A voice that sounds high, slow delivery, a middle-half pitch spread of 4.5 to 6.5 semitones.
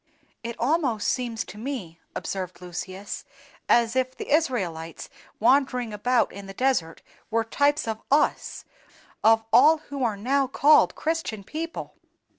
Yes: high, 235 Hz; slow, 130 wpm; average, 5.3 semitones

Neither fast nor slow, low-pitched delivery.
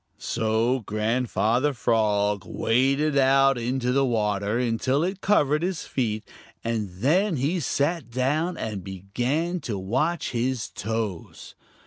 No: slow, 120 wpm; low, 125 Hz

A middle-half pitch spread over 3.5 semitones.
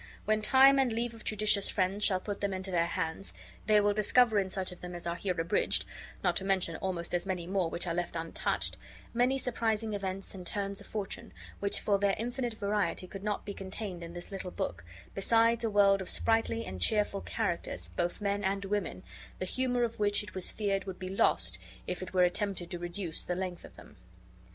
No: average, 2.8 semitones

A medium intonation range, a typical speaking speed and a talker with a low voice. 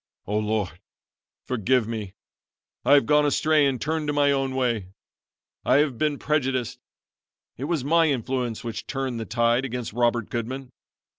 Yes: average, 3.5 semitones; average, 155 wpm; low, 130 Hz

